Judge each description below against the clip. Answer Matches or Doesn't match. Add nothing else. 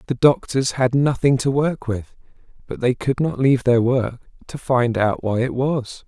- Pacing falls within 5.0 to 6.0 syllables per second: Doesn't match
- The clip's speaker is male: Matches